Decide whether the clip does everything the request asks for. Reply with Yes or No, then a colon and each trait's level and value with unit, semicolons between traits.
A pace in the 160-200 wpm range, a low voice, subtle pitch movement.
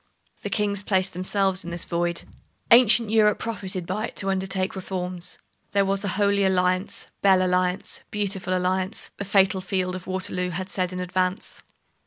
No: average, 165 wpm; high, 190 Hz; narrow, 1.5 semitones